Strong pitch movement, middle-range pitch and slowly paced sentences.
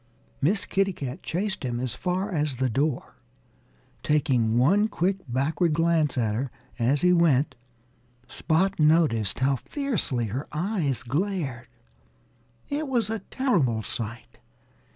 Yes: wide, 6.9 semitones; medium, 150 Hz; slow, 130 wpm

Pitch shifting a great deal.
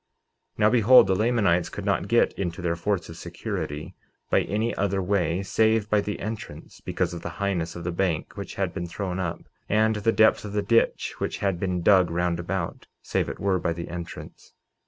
No: average, 3.2 semitones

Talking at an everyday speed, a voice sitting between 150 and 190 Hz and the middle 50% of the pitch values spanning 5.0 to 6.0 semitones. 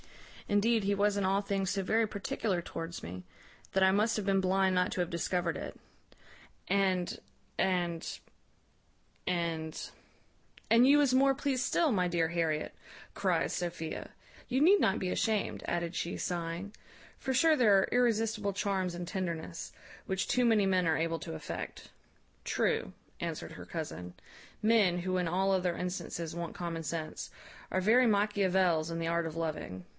No: average, 165 wpm; medium, 185 Hz; average, 3.4 semitones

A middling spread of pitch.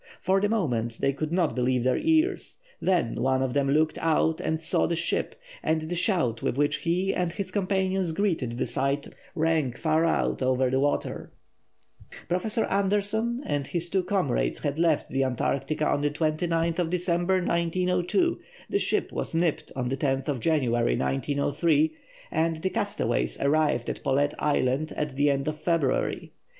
Yes: average, 4.7 semitones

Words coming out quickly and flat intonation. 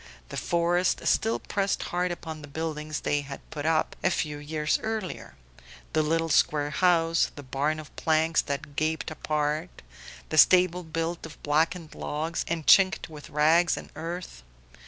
No: average, 155 wpm; narrow, 2.2 semitones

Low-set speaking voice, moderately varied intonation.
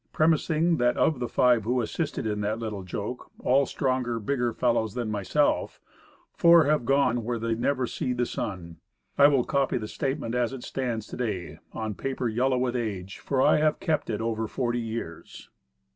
Yes: low, 120 Hz; average, 3.3 semitones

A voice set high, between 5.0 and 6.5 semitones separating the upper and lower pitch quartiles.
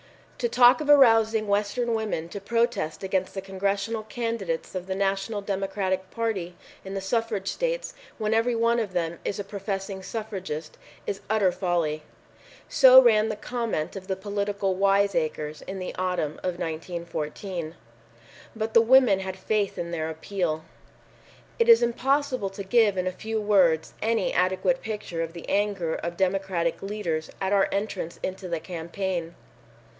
No: high, 195 Hz; average, 3.4 semitones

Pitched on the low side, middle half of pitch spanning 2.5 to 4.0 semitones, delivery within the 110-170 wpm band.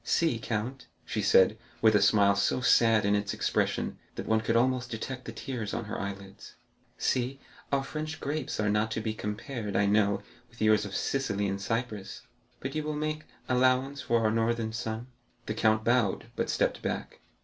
No: low, 110 Hz; average, 3.5 semitones; average, 180 wpm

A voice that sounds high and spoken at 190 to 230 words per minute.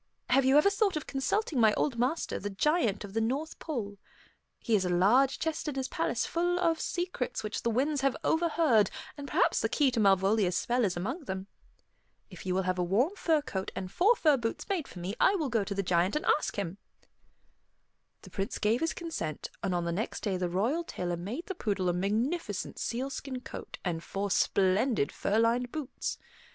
Yes: high, 230 Hz; fast, 205 wpm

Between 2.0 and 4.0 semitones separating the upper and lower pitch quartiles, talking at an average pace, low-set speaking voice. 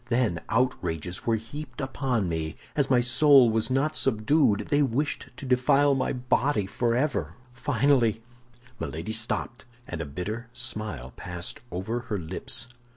No: average, 4.7 semitones; average, 145 wpm; low, 120 Hz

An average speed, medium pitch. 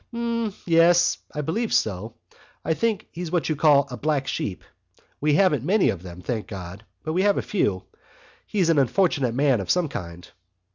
Yes: average, 180 wpm; medium, 150 Hz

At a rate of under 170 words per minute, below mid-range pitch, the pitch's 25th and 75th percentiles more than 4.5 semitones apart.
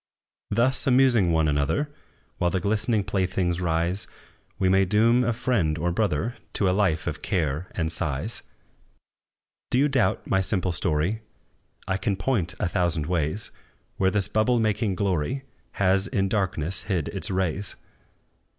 No: average, 150 wpm; very low, 95 Hz; average, 4.0 semitones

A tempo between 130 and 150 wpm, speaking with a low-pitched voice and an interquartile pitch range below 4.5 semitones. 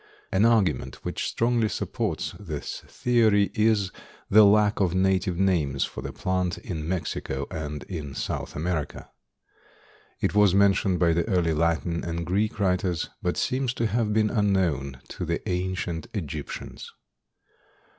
Yes: average, 140 wpm; very low, 95 Hz; average, 4.0 semitones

